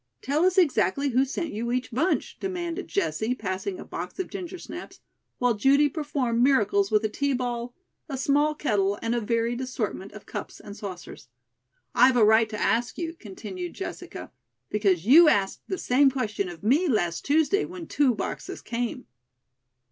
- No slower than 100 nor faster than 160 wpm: No, average, 175 wpm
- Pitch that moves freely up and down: Yes, wide, 5.8 semitones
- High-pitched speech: Yes, high, 245 Hz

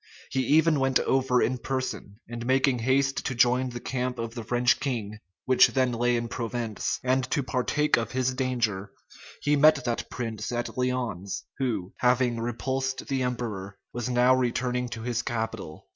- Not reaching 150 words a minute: No, average, 170 wpm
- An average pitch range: No, narrow, 1.9 semitones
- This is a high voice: No, low, 125 Hz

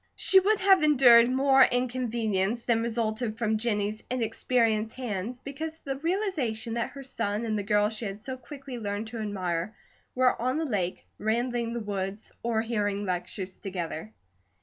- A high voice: Yes, high, 230 Hz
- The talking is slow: No, average, 165 wpm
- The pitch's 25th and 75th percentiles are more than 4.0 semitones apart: No, average, 3.5 semitones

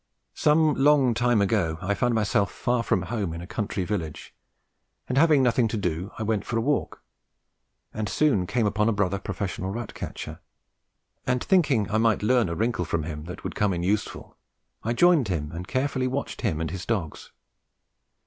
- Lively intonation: No, average, 5.0 semitones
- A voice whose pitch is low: Yes, low, 105 Hz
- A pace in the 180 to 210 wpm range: Yes, average, 185 wpm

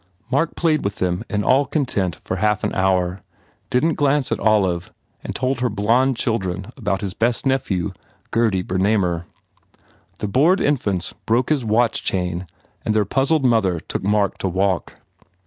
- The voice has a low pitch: Yes, low, 105 Hz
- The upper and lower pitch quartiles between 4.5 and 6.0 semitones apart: Yes, wide, 5.4 semitones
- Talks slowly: No, average, 165 wpm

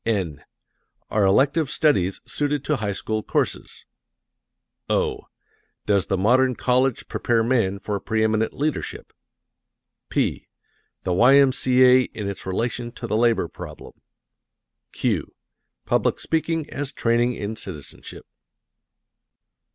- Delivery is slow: Yes, slow, 110 wpm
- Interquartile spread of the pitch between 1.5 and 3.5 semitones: No, average, 4.3 semitones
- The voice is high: No, low, 115 Hz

